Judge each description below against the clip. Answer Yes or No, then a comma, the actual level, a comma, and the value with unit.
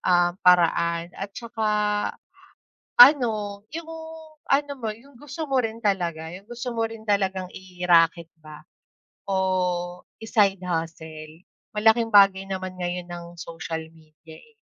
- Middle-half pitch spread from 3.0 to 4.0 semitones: No, average, 4.6 semitones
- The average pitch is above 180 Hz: Yes, high, 190 Hz